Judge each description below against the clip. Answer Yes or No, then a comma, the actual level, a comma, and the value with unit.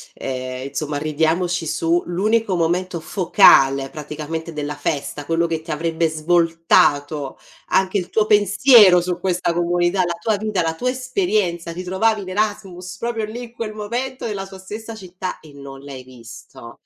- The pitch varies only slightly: No, average, 4.8 semitones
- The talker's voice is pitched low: No, medium, 175 Hz